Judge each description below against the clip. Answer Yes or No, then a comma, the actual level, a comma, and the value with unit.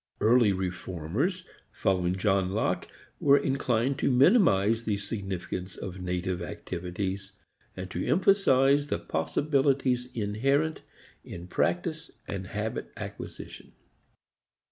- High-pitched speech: No, low, 105 Hz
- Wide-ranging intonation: Yes, wide, 6.8 semitones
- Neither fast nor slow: No, slow, 100 wpm